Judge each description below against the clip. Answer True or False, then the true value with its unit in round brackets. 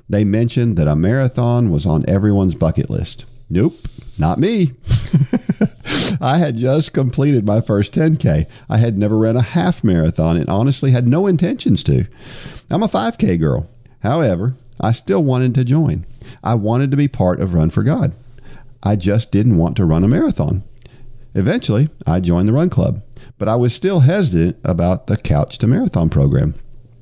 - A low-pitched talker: True (120 Hz)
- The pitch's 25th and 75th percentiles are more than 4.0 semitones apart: True (5.1 semitones)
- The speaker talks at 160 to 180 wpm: True (170 wpm)